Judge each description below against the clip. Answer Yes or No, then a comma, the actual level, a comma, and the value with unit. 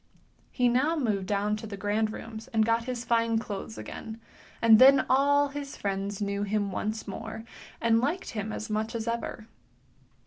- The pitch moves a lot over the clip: No, narrow, 2.4 semitones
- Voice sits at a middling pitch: No, high, 225 Hz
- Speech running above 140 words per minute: Yes, average, 175 wpm